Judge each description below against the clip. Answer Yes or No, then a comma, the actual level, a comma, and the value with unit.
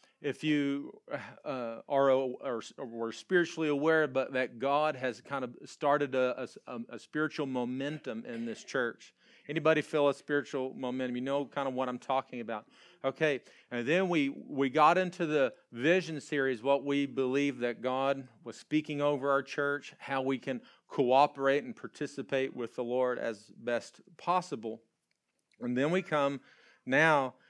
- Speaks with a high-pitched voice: No, medium, 140 Hz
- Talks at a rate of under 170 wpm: Yes, average, 160 wpm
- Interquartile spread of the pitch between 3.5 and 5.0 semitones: No, average, 2.7 semitones